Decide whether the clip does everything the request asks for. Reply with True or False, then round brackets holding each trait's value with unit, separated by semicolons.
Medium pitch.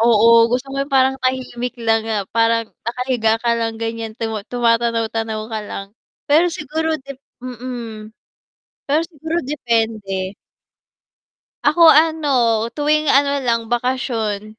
False (240 Hz)